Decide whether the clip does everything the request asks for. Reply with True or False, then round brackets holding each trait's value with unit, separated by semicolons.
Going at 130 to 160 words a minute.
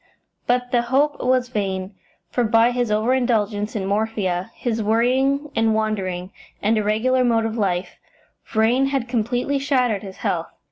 True (150 wpm)